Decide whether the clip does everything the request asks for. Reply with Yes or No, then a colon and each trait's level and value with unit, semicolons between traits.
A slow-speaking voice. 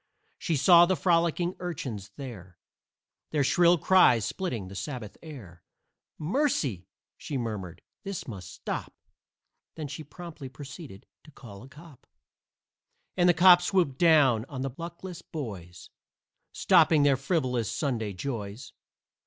Yes: slow, 125 wpm